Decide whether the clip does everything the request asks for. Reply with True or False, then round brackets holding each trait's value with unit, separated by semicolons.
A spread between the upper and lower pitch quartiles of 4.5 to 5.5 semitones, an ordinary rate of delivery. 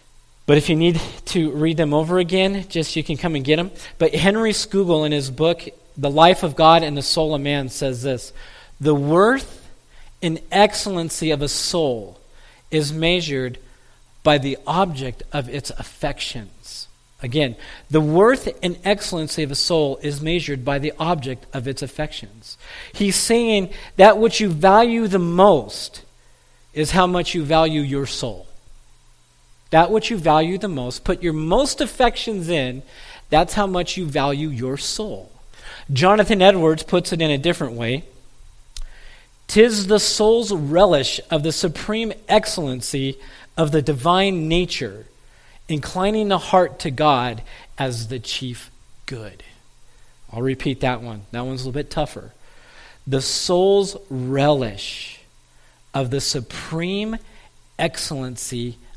True (5.1 semitones; 145 wpm)